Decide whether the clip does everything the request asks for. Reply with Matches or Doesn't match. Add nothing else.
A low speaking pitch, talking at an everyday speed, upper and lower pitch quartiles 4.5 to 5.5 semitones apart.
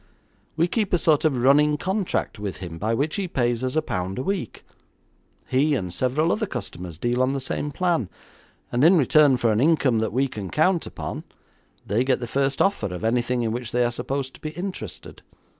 Doesn't match